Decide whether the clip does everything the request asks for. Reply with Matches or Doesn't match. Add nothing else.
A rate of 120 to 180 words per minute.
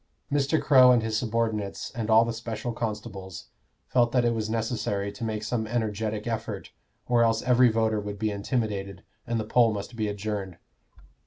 Matches